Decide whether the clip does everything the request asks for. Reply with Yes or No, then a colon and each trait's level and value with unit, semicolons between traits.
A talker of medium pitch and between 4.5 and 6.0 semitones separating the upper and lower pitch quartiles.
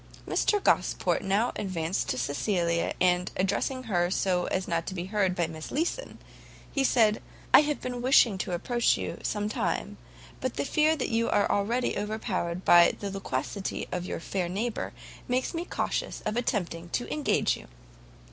No: high, 200 Hz; wide, 5.4 semitones